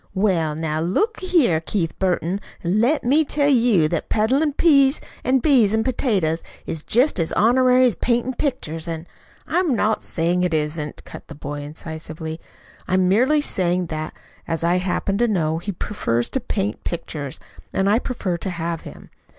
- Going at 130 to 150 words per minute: No, average, 175 wpm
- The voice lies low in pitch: No, high, 190 Hz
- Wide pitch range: Yes, wide, 7.3 semitones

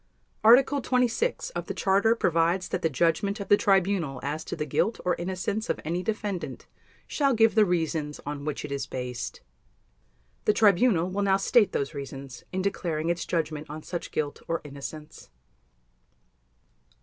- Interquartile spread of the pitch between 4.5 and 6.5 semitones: Yes, average, 5.1 semitones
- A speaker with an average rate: Yes, average, 160 wpm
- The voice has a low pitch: No, medium, 175 Hz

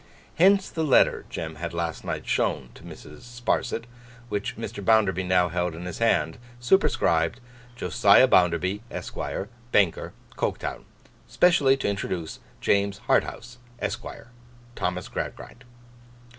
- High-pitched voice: No, low, 100 Hz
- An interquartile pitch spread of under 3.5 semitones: No, wide, 5.6 semitones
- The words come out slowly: Yes, slow, 120 wpm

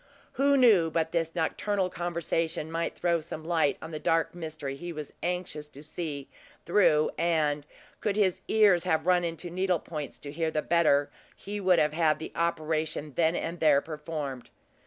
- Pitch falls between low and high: Yes, medium, 165 Hz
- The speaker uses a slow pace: No, average, 175 wpm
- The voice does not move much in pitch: Yes, narrow, 2.3 semitones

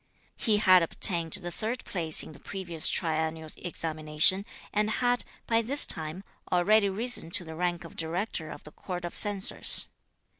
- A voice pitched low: No, medium, 175 Hz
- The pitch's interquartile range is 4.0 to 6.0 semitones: Yes, average, 4.3 semitones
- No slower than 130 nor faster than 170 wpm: Yes, average, 160 wpm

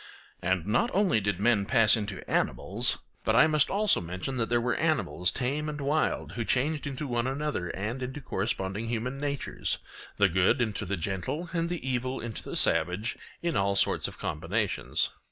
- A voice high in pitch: No, low, 120 Hz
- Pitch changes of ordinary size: No, wide, 6.2 semitones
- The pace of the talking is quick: No, average, 175 wpm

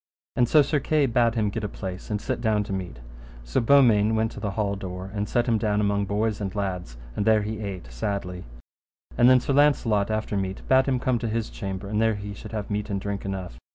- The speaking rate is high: Yes, fast, 240 wpm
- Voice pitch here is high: No, low, 105 Hz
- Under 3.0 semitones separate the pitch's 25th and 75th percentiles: Yes, narrow, 2.6 semitones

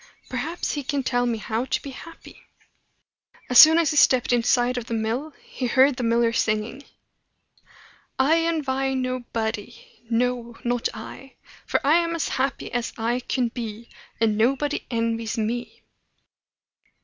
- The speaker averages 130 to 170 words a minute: Yes, average, 150 wpm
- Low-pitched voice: No, high, 245 Hz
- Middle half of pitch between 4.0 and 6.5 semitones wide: No, average, 2.9 semitones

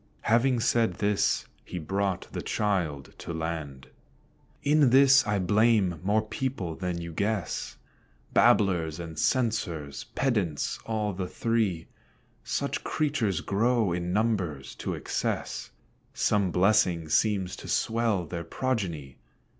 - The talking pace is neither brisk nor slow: No, slow, 120 wpm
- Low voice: Yes, low, 100 Hz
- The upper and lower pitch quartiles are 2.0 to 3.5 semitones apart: No, average, 4.9 semitones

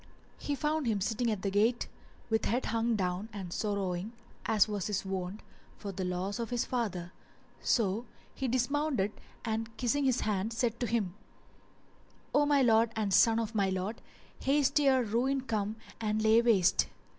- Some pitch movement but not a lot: Yes, average, 3.4 semitones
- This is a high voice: Yes, high, 220 Hz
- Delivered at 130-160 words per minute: No, average, 170 wpm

